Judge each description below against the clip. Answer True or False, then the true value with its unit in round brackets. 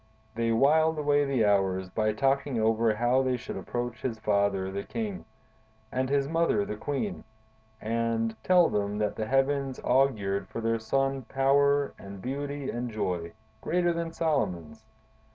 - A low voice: True (120 Hz)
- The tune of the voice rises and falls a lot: False (4.7 semitones)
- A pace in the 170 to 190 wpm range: False (155 wpm)